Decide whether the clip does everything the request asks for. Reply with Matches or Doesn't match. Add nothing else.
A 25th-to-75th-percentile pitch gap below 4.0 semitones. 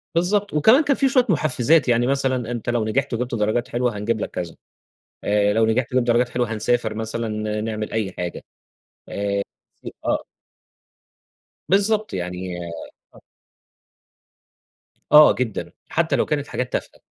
Doesn't match